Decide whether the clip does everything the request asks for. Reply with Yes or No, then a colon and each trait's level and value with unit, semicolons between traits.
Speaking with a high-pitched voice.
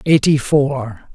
No: low, 135 Hz